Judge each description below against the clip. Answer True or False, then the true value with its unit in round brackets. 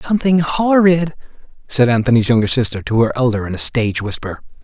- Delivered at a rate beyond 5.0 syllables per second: True (6.3 syllables/s)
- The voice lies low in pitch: True (130 Hz)